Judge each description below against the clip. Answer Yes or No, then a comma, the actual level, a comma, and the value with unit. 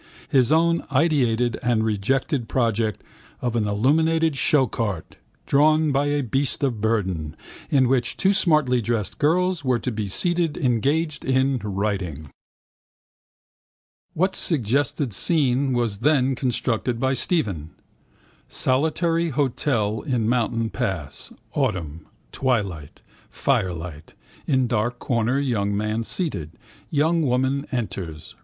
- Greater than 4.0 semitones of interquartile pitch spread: Yes, average, 5.2 semitones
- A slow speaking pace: Yes, slow, 115 wpm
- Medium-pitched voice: No, low, 125 Hz